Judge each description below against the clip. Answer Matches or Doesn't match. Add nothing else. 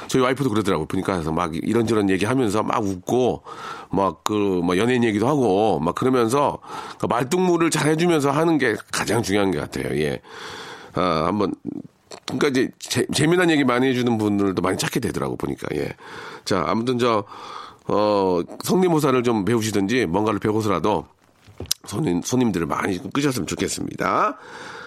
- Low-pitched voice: Matches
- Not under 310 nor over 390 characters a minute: Matches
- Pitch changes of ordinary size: Doesn't match